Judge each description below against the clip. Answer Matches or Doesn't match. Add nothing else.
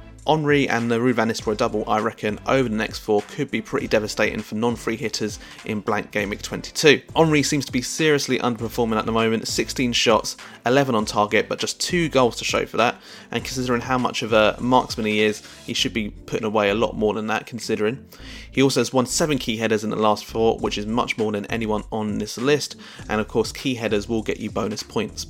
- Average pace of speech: Doesn't match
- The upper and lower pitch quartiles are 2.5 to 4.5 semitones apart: Matches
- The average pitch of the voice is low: Matches